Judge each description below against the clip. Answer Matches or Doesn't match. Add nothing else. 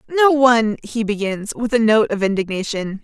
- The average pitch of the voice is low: Doesn't match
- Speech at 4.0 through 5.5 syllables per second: Matches